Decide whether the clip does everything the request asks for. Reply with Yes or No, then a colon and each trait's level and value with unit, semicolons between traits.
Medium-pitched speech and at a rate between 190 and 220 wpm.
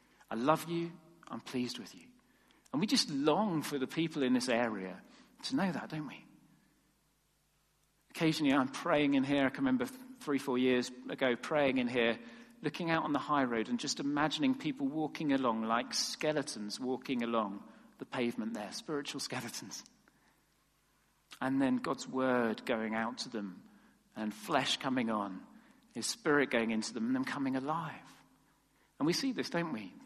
No: medium, 145 Hz; average, 170 wpm